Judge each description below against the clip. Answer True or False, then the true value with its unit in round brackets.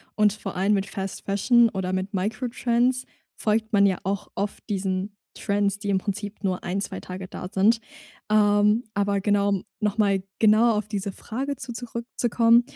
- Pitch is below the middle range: False (205 Hz)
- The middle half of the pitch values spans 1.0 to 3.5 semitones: True (2.4 semitones)